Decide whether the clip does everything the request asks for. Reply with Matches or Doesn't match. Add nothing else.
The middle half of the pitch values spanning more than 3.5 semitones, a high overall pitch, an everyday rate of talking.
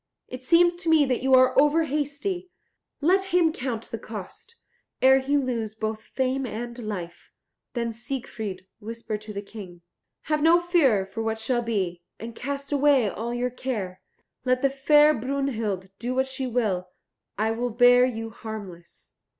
Matches